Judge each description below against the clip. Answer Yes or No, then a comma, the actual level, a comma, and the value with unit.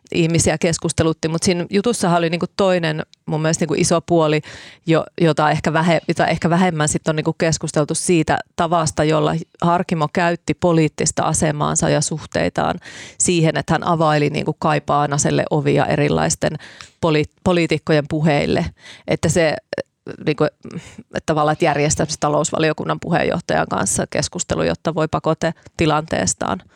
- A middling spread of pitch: No, narrow, 2.0 semitones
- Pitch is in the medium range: Yes, medium, 160 Hz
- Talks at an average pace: Yes, average, 135 wpm